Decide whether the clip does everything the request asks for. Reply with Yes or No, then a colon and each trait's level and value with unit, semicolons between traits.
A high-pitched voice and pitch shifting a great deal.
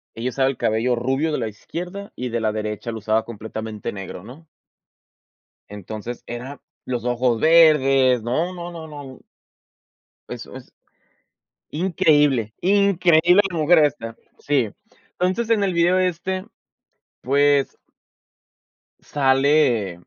No: low, 135 Hz; wide, 6.4 semitones